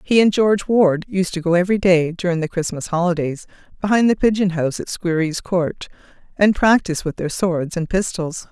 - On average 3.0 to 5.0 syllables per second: No, 5.6 syllables/s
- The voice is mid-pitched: Yes, medium, 180 Hz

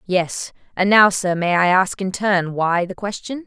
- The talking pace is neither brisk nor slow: No, fast, 210 wpm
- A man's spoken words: No, female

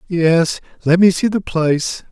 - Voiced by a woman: No, male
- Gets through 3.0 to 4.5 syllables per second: Yes, 4.2 syllables/s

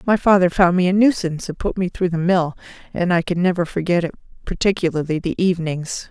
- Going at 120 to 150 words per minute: No, fast, 205 wpm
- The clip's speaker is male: No, female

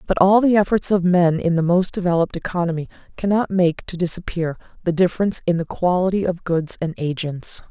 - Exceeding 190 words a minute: No, average, 185 wpm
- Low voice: No, medium, 175 Hz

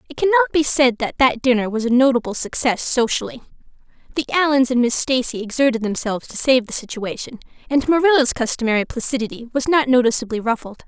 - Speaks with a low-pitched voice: No, very high, 250 Hz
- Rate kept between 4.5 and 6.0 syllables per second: No, 6.6 syllables/s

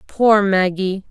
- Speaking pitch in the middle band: No, high, 195 Hz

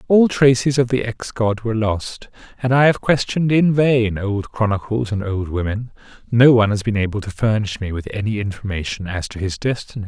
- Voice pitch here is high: No, low, 110 Hz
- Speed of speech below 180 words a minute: No, fast, 205 wpm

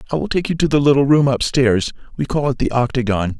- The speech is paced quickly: Yes, fast, 245 wpm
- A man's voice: Yes, male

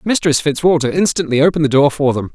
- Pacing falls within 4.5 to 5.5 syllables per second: No, 6.7 syllables/s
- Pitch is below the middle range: No, medium, 150 Hz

